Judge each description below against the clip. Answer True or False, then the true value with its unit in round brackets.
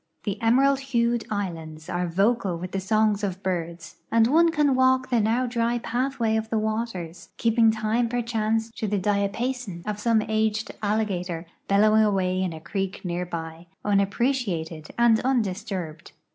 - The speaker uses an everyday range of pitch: True (4.2 semitones)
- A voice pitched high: True (215 Hz)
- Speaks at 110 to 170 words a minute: True (160 wpm)